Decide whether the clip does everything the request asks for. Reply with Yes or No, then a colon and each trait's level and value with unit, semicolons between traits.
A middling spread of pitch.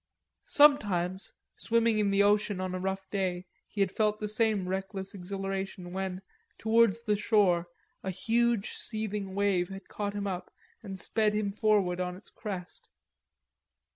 No: narrow, 2.2 semitones